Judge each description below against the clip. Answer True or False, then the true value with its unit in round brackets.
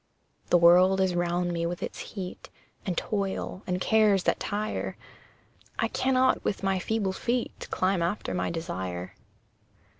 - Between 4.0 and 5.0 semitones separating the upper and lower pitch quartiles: False (2.8 semitones)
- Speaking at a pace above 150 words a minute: False (145 wpm)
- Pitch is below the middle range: False (185 Hz)